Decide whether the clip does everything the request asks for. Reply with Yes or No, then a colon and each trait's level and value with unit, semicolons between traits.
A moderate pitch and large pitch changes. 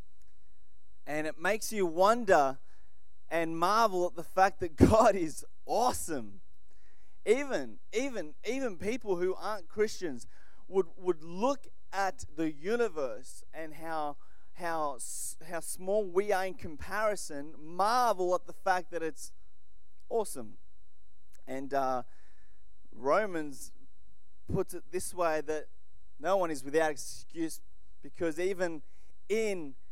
Yes: medium, 165 Hz; wide, 7.2 semitones